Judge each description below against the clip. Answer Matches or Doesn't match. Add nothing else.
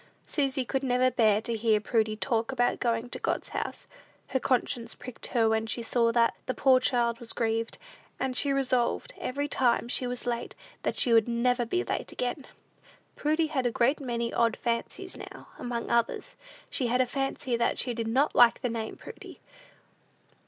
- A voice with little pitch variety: Matches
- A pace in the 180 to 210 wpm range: Matches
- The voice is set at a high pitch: Matches